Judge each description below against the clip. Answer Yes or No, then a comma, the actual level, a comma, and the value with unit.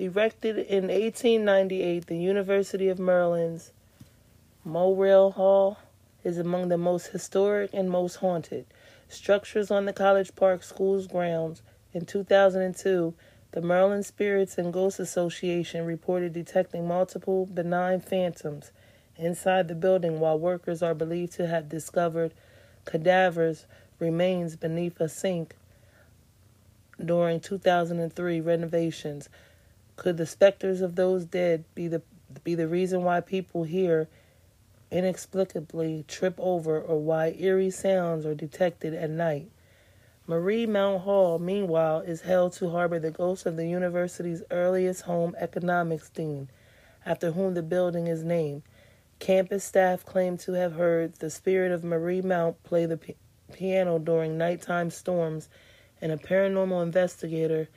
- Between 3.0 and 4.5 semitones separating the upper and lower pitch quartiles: No, narrow, 2.5 semitones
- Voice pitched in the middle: Yes, medium, 175 Hz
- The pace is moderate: No, slow, 130 wpm